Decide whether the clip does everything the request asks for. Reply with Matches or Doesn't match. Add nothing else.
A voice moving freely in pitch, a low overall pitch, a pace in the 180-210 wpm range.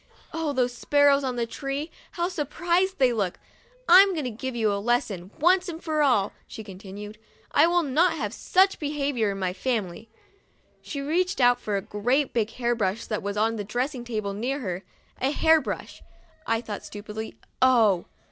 Doesn't match